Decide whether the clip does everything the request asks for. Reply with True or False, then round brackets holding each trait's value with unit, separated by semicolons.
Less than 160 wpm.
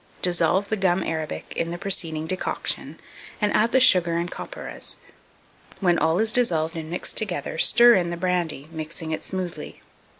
False (165 wpm)